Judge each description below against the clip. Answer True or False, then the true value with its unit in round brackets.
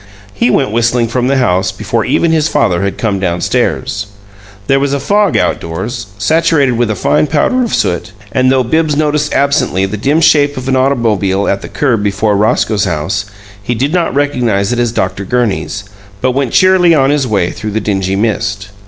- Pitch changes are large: True (6.0 semitones)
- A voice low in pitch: True (120 Hz)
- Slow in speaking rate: False (195 wpm)